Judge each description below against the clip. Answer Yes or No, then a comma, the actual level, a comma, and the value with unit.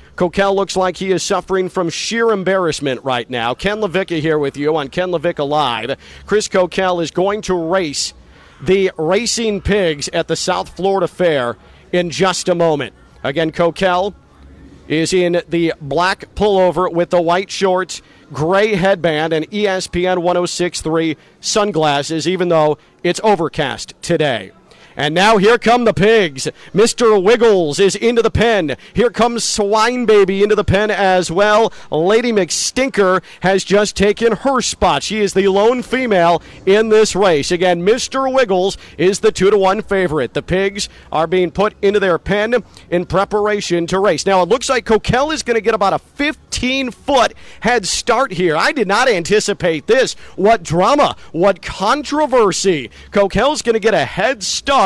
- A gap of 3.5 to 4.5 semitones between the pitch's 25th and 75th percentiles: Yes, average, 3.8 semitones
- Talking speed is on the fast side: No, average, 165 wpm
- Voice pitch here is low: No, high, 190 Hz